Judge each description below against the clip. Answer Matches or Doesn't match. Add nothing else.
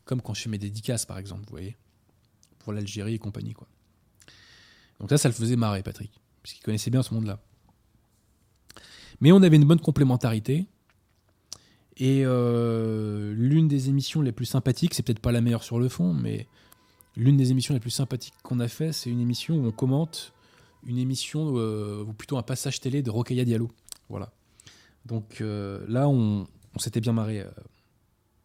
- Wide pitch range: Doesn't match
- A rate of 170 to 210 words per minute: Matches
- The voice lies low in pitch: Matches